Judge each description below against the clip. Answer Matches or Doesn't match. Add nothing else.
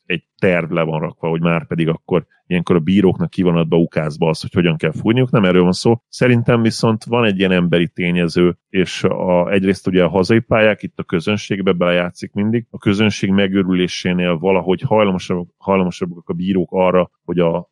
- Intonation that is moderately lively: Matches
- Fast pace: Matches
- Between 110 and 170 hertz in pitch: Doesn't match